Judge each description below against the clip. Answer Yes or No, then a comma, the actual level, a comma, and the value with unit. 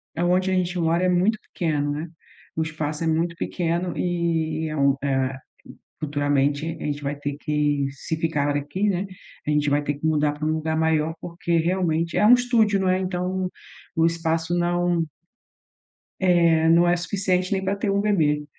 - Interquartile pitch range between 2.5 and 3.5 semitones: Yes, average, 3.2 semitones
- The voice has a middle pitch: Yes, medium, 165 Hz